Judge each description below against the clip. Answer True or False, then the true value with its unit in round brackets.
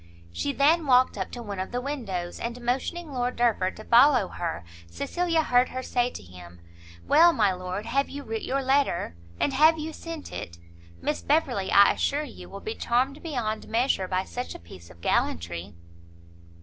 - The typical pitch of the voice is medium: False (245 Hz)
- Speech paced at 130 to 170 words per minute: False (185 wpm)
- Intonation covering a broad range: True (7.0 semitones)